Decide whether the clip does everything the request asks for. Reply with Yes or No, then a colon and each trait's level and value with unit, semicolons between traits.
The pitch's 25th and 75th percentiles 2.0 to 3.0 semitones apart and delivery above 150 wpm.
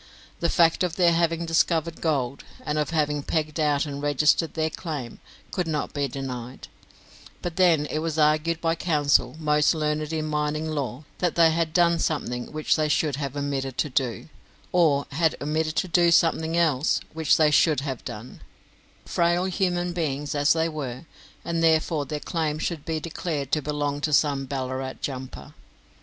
Yes: narrow, 2.5 semitones; average, 175 wpm